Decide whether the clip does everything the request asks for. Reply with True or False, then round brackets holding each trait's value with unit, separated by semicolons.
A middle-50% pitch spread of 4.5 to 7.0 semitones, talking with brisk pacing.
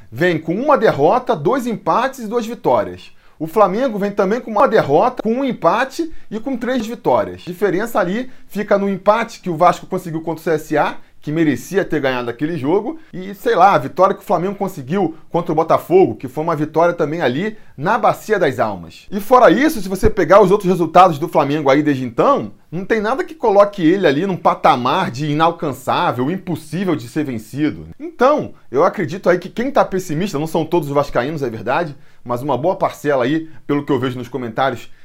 True (5.6 semitones; 205 wpm)